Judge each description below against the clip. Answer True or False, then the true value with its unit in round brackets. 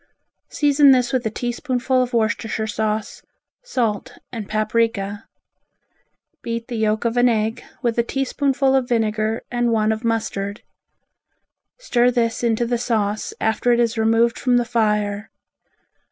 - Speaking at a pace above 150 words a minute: False (140 wpm)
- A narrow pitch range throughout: True (2.0 semitones)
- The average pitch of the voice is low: False (230 Hz)